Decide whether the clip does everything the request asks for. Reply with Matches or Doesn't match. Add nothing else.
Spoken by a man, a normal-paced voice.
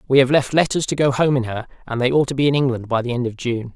Doesn't match